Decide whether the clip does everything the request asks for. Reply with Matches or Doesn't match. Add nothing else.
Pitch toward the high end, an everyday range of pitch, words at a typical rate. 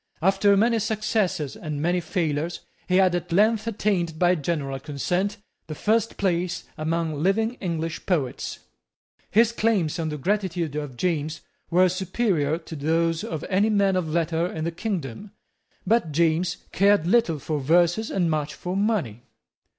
Doesn't match